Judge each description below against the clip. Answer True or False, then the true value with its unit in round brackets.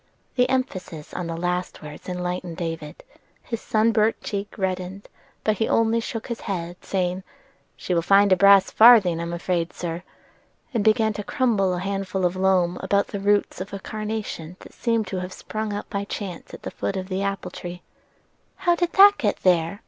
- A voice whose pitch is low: False (195 Hz)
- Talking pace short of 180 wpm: False (185 wpm)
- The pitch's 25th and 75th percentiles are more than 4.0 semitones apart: False (3.2 semitones)